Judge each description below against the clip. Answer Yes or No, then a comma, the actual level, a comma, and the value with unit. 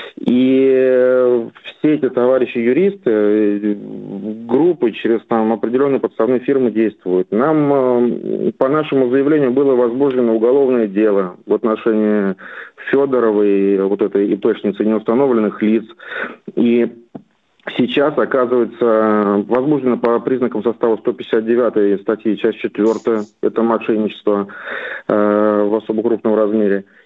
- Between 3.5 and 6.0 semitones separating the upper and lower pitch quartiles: No, average, 3.0 semitones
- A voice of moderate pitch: No, low, 115 Hz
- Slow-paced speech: Yes, slow, 105 wpm